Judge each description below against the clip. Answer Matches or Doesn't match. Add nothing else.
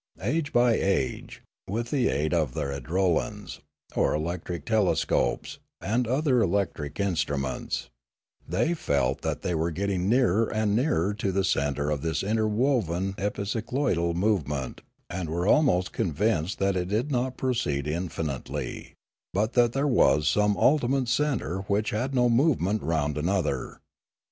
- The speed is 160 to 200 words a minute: Doesn't match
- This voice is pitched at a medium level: Doesn't match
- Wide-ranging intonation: Matches